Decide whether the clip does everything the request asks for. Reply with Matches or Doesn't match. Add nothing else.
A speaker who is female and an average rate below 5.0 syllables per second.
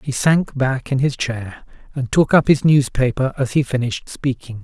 Doesn't match